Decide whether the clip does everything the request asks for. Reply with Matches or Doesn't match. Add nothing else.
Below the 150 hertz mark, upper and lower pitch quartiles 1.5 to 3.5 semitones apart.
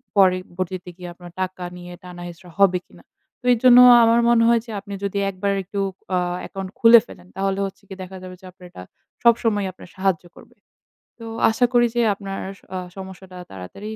Doesn't match